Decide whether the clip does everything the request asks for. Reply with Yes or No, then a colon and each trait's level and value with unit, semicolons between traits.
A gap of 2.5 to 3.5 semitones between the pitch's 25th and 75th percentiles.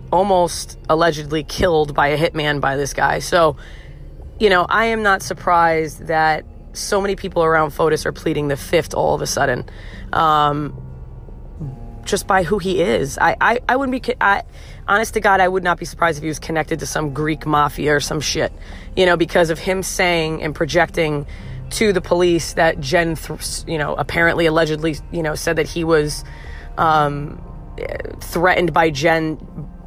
Yes: average, 3.1 semitones